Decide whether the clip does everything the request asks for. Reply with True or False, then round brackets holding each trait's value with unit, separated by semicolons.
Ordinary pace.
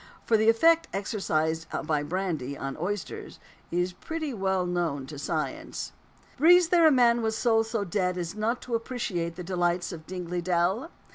True (165 wpm)